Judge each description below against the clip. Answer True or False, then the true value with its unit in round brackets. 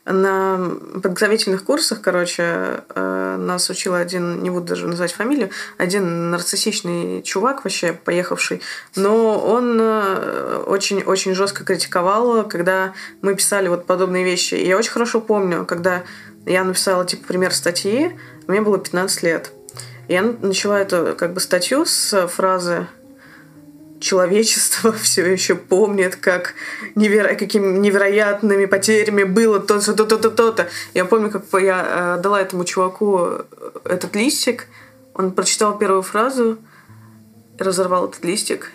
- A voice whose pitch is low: False (190 Hz)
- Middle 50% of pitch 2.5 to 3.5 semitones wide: True (3.0 semitones)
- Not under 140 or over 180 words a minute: False (125 wpm)